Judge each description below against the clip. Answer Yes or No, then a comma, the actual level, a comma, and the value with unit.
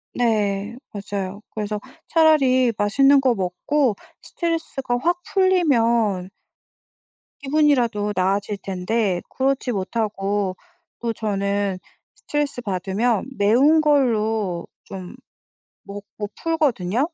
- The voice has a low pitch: No, high, 220 Hz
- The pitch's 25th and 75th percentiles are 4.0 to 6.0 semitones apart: Yes, average, 5.3 semitones